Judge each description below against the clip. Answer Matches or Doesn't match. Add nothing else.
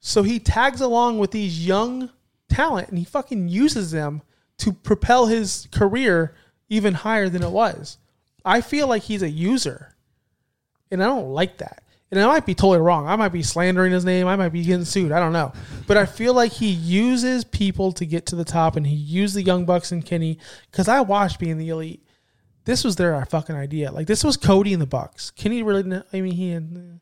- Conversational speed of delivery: Doesn't match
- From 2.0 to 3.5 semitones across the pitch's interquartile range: Doesn't match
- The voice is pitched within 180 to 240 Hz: Matches